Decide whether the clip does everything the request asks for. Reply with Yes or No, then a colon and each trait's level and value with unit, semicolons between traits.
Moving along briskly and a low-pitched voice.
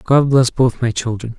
Yes: fast, 215 wpm; low, 125 Hz